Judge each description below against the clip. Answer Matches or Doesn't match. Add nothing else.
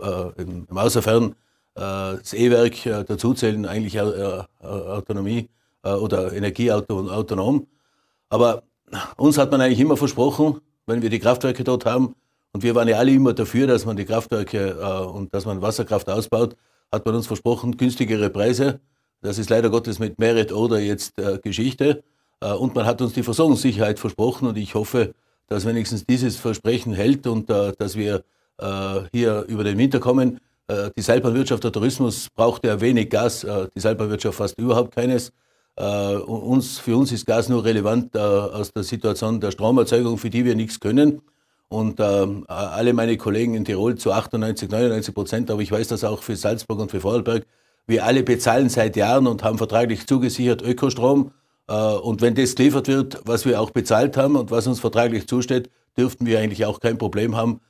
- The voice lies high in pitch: Doesn't match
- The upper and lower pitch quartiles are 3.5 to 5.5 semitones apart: Doesn't match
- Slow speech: Doesn't match